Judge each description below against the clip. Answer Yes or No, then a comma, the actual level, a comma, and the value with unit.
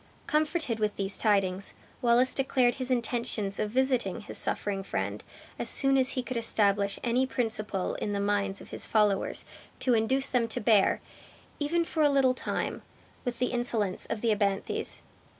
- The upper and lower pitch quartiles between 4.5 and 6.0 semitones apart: No, average, 4.0 semitones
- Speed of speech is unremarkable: Yes, average, 170 wpm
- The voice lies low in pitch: No, high, 230 Hz